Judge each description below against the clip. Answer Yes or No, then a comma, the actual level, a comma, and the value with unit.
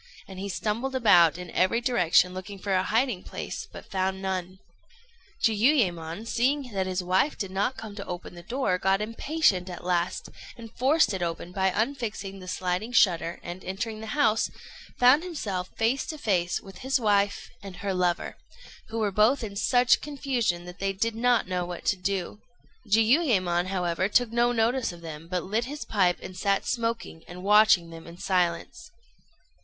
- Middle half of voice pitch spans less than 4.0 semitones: No, average, 4.3 semitones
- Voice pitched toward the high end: Yes, high, 200 Hz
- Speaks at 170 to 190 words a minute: Yes, average, 180 wpm